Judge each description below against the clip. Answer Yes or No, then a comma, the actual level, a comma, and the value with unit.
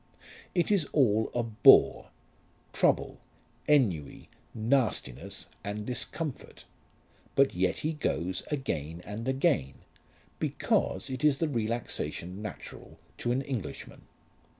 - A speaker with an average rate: No, slow, 105 wpm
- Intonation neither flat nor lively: No, wide, 6.5 semitones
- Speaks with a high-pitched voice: No, low, 115 Hz